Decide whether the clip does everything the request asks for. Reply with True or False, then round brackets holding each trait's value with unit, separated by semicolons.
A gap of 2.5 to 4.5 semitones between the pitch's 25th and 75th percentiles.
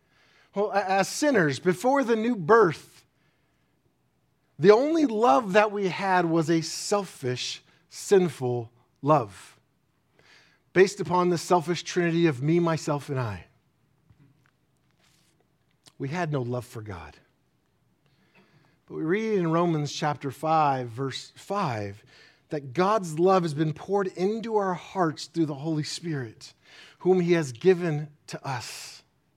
False (5.1 semitones)